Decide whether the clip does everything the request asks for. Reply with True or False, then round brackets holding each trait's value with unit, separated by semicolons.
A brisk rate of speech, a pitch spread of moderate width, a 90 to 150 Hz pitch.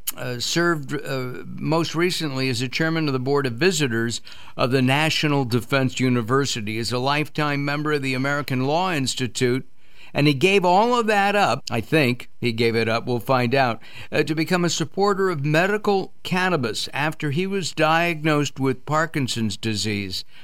False (170 wpm; 4.4 semitones; 140 Hz)